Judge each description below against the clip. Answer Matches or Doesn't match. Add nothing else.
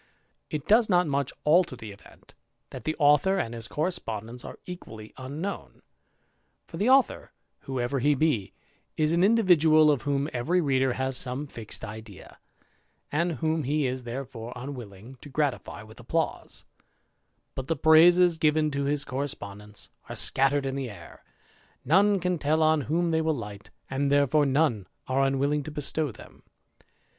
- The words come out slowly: Doesn't match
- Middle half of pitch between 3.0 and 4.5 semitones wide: Matches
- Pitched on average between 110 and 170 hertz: Matches